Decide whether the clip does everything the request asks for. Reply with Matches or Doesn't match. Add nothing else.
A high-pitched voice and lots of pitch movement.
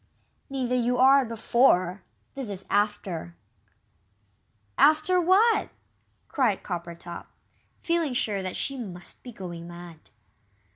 Matches